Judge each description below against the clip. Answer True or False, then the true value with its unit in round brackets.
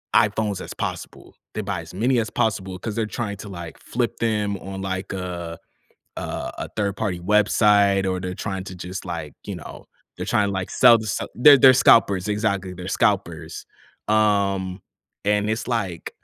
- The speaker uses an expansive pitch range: False (2.6 semitones)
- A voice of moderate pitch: False (100 Hz)